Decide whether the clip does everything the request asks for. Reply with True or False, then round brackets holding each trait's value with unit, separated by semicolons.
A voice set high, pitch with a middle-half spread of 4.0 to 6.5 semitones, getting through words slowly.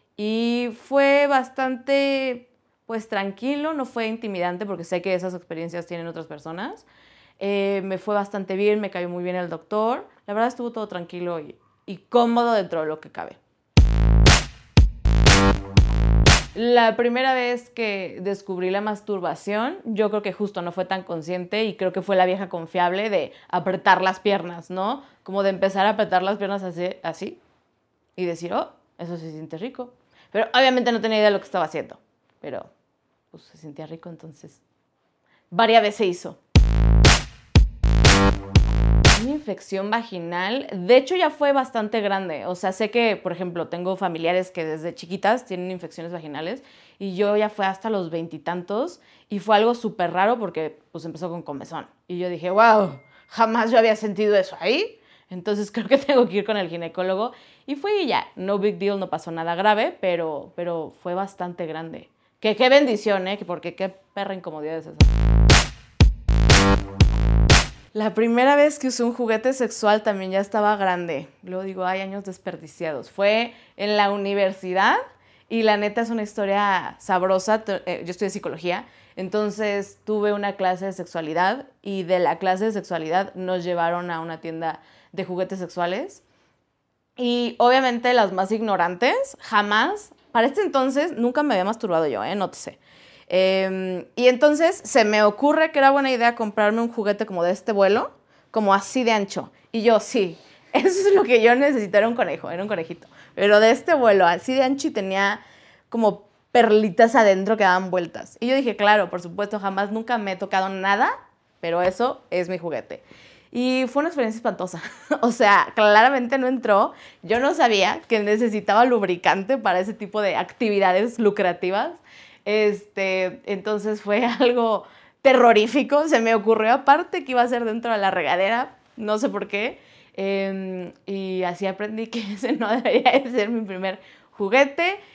False (205 Hz; 4.3 semitones; 170 wpm)